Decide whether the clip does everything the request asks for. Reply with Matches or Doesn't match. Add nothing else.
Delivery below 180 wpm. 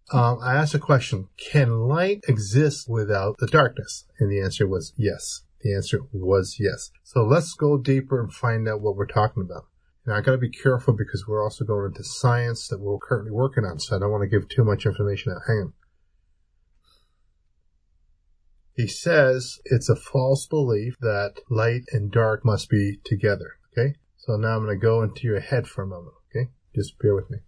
Doesn't match